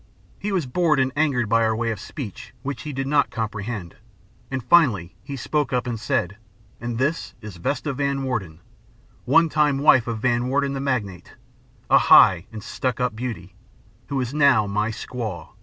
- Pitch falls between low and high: No, low, 125 Hz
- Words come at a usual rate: Yes, average, 180 wpm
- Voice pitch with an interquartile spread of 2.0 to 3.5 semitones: No, average, 4.3 semitones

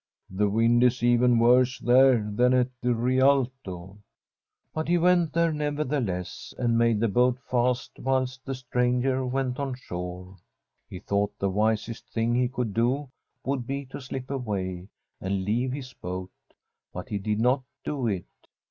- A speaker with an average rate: Yes, average, 160 wpm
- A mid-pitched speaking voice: No, low, 125 Hz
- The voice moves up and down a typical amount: Yes, average, 3.7 semitones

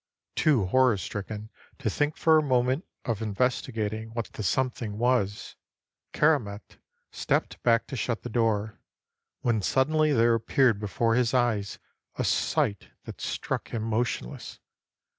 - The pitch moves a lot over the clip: No, average, 3.3 semitones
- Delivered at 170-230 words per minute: No, slow, 135 wpm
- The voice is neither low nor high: No, low, 115 Hz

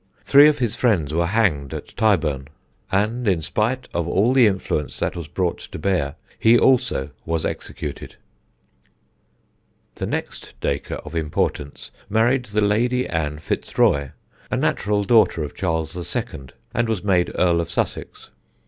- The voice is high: No, very low, 95 Hz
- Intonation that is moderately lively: No, wide, 6.1 semitones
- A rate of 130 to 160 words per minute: Yes, average, 150 wpm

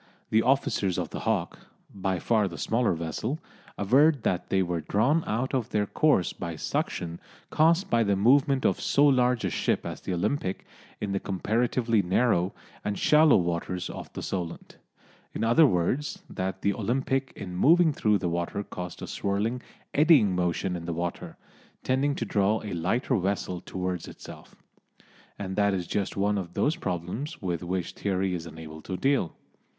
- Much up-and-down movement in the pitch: Yes, wide, 5.9 semitones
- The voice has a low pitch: Yes, low, 100 Hz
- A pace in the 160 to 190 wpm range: Yes, average, 170 wpm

